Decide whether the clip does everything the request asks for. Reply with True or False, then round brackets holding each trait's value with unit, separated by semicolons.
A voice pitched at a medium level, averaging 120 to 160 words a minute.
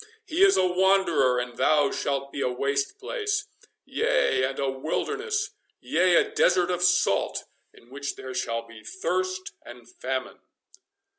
True (155 Hz; 140 wpm)